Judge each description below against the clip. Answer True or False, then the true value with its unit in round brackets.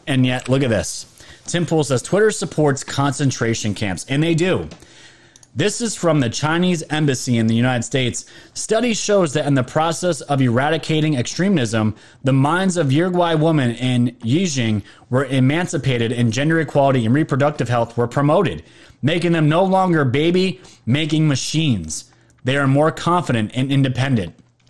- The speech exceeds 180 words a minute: False (155 wpm)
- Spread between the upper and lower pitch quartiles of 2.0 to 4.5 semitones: False (5.0 semitones)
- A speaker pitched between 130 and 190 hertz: True (140 Hz)